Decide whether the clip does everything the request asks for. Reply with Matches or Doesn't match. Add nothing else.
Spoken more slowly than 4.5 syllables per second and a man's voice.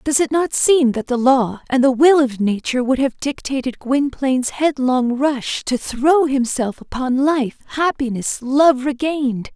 Doesn't match